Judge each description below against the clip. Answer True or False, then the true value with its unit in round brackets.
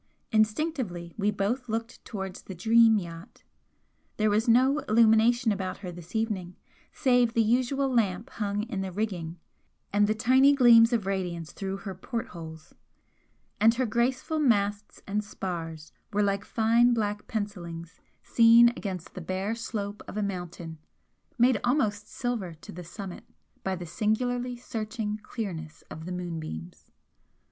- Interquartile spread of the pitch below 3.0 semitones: False (4.2 semitones)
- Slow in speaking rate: False (145 wpm)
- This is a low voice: False (210 Hz)